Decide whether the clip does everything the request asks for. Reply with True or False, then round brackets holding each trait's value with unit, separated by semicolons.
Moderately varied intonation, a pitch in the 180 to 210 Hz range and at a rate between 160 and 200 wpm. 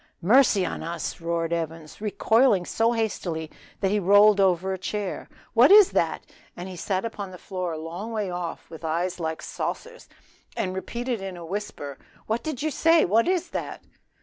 True (4.6 semitones; 190 Hz; 165 wpm)